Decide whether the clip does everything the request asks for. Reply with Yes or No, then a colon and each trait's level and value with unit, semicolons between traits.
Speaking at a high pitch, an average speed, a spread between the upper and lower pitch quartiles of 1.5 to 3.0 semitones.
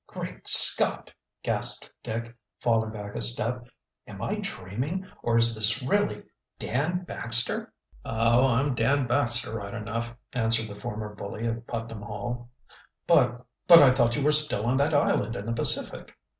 No: low, 120 Hz; average, 155 wpm; narrow, 2.5 semitones